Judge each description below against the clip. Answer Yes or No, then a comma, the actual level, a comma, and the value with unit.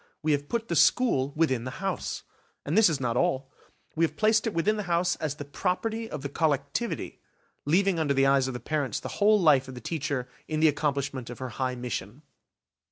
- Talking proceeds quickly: Yes, fast, 215 wpm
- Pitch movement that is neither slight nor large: Yes, average, 5.0 semitones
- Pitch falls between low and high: Yes, medium, 145 Hz